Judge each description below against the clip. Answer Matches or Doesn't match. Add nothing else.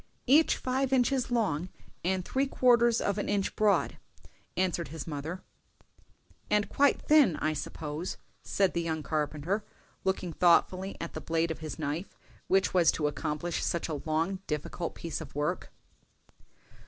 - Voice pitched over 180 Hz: Doesn't match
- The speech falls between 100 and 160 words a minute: Matches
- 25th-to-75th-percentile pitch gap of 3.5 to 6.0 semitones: Matches